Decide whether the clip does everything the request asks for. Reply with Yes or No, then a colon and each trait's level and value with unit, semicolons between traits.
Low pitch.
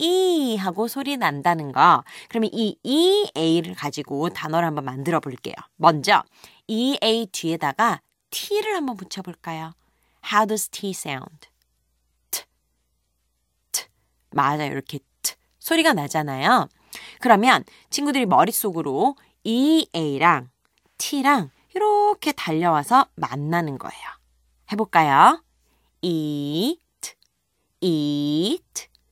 No: medium, 170 Hz